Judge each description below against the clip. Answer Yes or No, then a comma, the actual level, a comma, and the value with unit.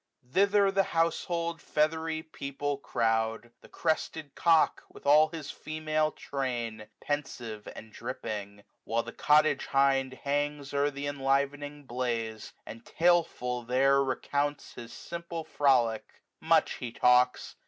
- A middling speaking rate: No, slow, 125 wpm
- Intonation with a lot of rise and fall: No, average, 3.9 semitones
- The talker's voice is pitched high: No, medium, 140 Hz